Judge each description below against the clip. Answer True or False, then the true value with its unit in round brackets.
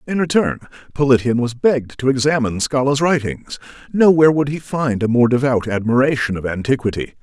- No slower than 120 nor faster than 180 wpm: True (160 wpm)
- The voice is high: False (130 Hz)